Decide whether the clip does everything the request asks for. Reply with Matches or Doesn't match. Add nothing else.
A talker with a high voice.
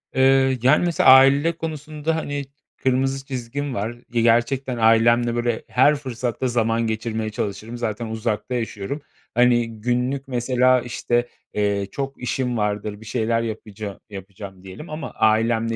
Doesn't match